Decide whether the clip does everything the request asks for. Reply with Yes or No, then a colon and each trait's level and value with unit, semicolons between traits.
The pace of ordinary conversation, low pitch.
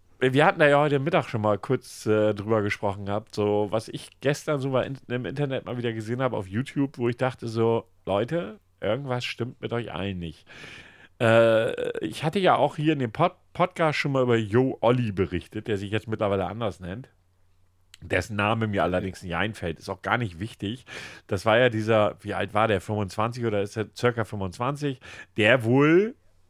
No: fast, 195 wpm; low, 115 Hz